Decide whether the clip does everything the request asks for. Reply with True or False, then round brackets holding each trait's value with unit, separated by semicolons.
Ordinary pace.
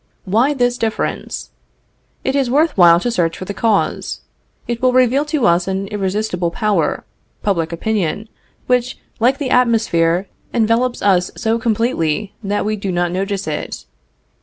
True (150 wpm)